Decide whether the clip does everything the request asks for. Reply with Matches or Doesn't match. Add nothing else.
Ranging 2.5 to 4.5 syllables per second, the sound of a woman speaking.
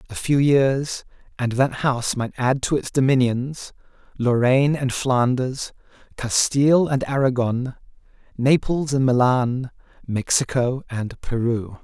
Doesn't match